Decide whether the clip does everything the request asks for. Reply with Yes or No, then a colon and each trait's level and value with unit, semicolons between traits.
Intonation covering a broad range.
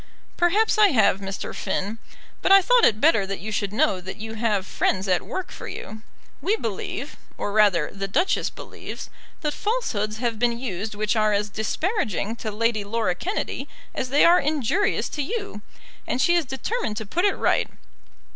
Yes: wide, 8.6 semitones